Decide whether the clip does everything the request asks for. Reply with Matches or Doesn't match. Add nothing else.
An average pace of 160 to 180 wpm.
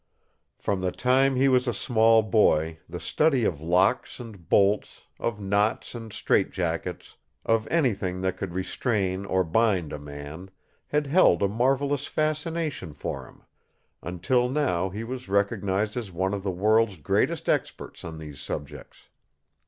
Doesn't match